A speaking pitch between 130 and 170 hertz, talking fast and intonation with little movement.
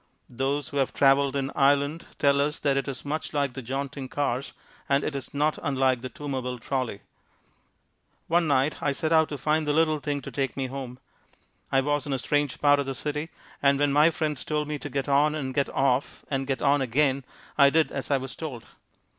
Yes: medium, 140 Hz; fast, 215 wpm; narrow, 1.6 semitones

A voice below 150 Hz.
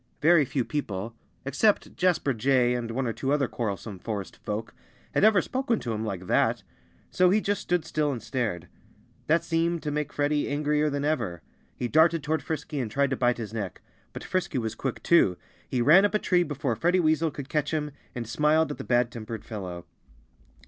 Yes: medium, 140 Hz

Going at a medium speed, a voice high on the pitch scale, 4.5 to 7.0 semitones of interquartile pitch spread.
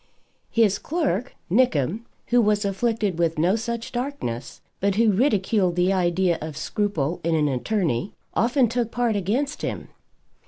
Yes: average, 145 wpm; high, 205 Hz; average, 5.3 semitones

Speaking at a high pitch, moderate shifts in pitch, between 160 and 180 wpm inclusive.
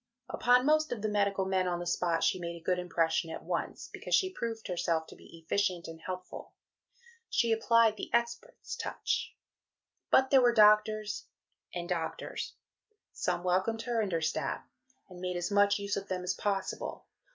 Yes: high, 195 Hz; average, 4.1 semitones; average, 175 wpm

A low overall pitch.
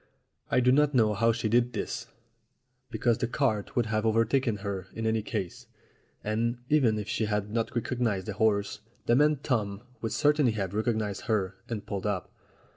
Yes: low, 110 Hz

